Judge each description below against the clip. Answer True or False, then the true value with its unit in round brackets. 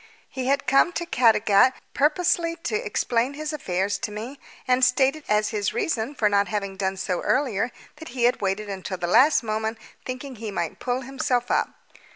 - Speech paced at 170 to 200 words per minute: True (185 wpm)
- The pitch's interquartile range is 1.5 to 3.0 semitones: False (4.9 semitones)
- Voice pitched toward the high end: True (240 Hz)